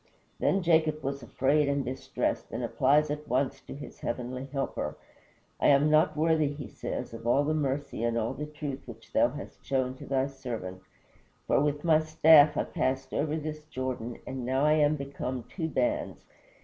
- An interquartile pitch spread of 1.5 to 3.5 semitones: Yes, average, 2.8 semitones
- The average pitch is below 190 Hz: Yes, medium, 140 Hz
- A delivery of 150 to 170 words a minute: No, average, 185 wpm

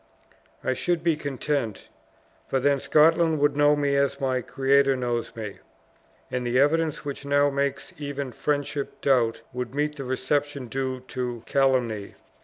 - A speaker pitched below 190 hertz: Yes, medium, 140 Hz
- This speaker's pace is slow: No, average, 150 wpm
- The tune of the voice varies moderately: No, narrow, 2.2 semitones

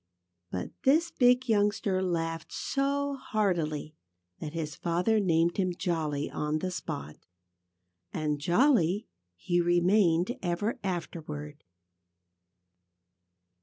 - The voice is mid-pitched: Yes, medium, 175 Hz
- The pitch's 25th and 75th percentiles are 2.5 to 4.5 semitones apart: No, average, 5.1 semitones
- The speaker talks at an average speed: No, slow, 95 wpm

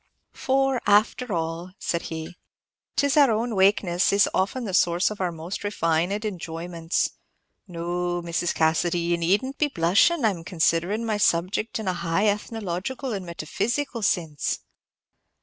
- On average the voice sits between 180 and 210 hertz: Yes, medium, 185 Hz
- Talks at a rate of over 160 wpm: No, average, 150 wpm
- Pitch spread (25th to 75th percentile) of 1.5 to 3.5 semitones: No, average, 4.3 semitones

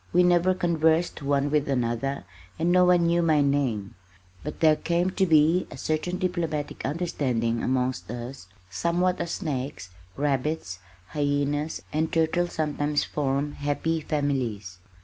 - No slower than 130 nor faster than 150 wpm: Yes, slow, 135 wpm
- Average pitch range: Yes, average, 3.7 semitones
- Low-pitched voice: No, medium, 150 Hz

